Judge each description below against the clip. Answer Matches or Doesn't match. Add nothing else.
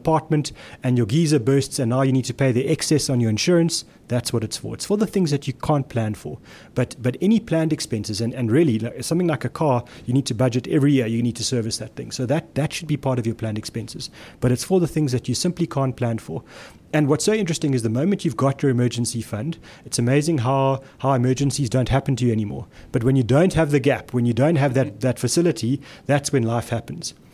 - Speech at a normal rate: Doesn't match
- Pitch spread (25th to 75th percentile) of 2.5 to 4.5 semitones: Matches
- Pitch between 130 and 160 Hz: Matches